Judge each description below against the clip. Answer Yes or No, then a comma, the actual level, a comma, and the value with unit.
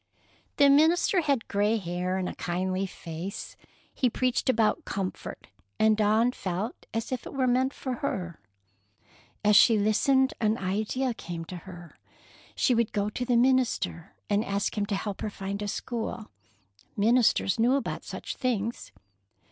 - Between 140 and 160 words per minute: Yes, average, 155 wpm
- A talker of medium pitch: No, high, 215 Hz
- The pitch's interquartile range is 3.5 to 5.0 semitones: Yes, average, 4.5 semitones